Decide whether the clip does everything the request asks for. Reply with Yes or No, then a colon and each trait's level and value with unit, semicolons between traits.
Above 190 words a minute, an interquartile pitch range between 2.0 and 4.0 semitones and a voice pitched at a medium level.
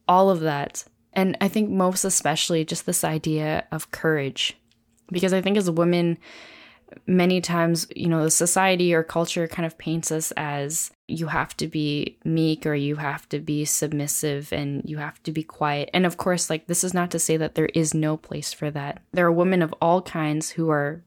Yes: fast, 205 wpm; narrow, 2.6 semitones; medium, 160 Hz